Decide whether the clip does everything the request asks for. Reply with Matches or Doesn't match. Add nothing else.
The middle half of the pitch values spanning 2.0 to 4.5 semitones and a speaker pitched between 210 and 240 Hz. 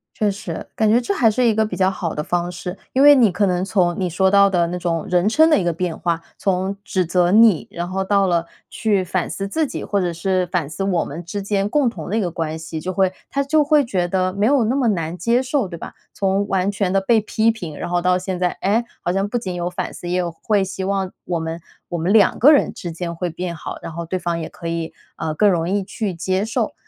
Doesn't match